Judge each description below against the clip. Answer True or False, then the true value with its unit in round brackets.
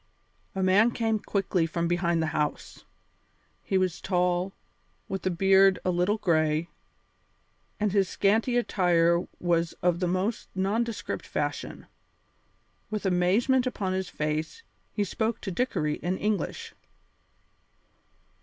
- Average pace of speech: False (125 wpm)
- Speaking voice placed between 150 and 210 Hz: True (185 Hz)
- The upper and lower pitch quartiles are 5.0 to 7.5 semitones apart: False (3.2 semitones)